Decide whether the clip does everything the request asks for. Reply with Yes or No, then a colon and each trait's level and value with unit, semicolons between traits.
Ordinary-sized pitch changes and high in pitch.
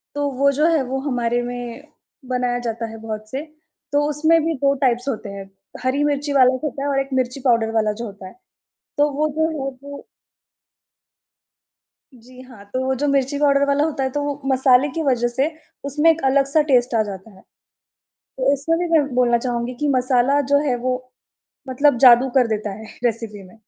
Yes: average, 3.0 semitones; very high, 260 Hz